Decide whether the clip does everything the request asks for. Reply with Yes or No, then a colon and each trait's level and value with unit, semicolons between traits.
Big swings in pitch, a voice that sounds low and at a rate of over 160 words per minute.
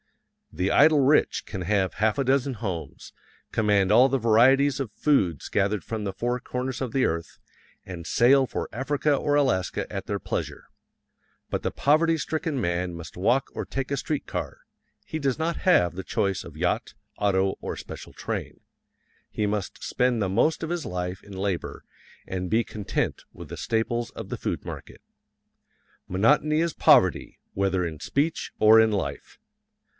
Yes: wide, 6.3 semitones; low, 115 Hz; average, 170 wpm